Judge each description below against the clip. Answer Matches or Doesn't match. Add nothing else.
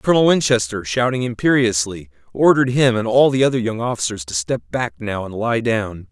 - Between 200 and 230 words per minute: Doesn't match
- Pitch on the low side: Matches